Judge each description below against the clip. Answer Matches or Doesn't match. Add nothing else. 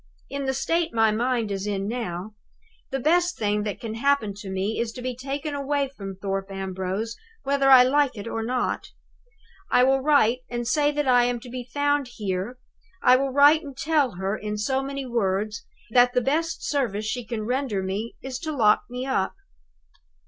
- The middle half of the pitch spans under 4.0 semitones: Doesn't match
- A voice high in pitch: Matches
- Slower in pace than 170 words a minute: Doesn't match